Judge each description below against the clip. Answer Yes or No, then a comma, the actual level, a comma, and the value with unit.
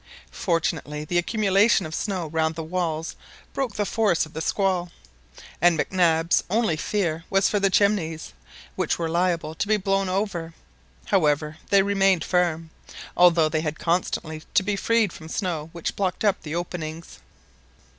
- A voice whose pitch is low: No, medium, 175 Hz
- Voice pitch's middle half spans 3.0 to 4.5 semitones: Yes, average, 3.4 semitones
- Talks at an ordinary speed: Yes, average, 165 wpm